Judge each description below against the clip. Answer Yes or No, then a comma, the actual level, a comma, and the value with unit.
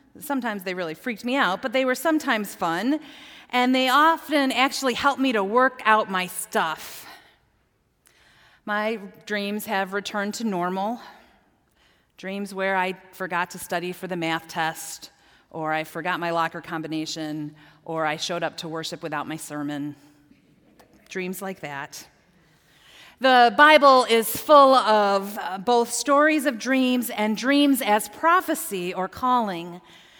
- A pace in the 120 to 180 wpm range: Yes, average, 140 wpm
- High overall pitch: Yes, high, 205 Hz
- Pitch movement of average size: No, wide, 6.8 semitones